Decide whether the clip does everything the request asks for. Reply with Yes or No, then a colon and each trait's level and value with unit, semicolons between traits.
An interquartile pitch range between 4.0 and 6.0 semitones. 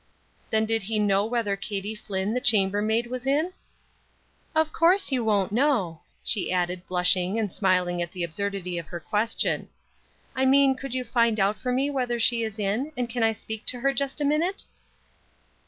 Yes: average, 4.7 semitones